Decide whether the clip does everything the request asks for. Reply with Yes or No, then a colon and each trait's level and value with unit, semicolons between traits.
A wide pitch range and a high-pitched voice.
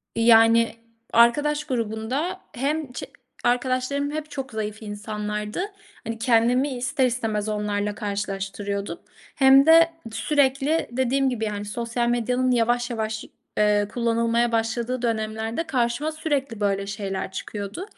No: average, 3.7 semitones; high, 235 Hz